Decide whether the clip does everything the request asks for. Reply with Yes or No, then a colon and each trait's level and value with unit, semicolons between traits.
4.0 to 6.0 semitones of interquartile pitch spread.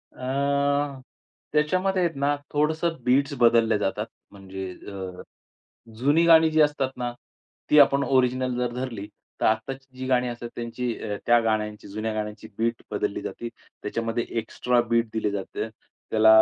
Yes: average, 4.3 semitones